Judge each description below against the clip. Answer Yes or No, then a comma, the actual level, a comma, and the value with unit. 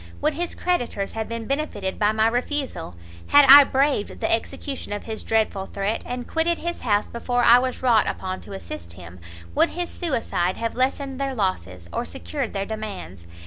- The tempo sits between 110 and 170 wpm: No, average, 185 wpm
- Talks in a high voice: Yes, high, 225 Hz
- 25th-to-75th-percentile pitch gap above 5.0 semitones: Yes, wide, 5.6 semitones